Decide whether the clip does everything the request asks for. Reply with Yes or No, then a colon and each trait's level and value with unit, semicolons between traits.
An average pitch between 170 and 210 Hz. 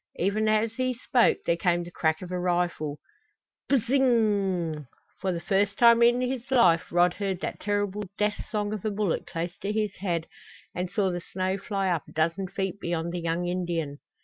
Yes: high, 190 Hz